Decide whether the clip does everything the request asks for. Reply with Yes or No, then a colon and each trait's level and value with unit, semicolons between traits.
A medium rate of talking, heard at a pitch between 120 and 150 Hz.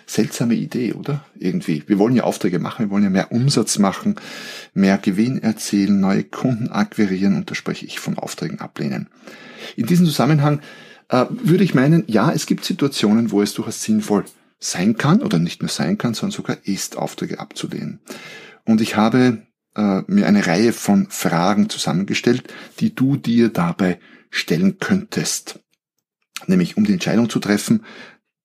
Yes: average, 160 wpm; low, 125 Hz